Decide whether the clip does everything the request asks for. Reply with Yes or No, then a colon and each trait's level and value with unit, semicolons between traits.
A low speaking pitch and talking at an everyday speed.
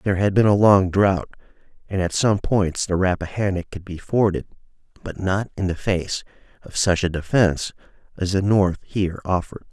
Yes: very low, 95 Hz; average, 180 wpm